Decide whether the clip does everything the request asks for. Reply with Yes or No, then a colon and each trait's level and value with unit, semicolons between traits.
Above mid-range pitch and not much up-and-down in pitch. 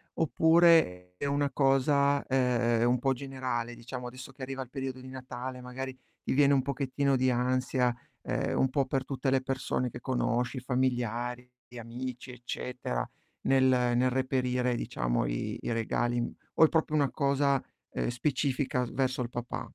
No: low, 130 Hz; narrow, 1.6 semitones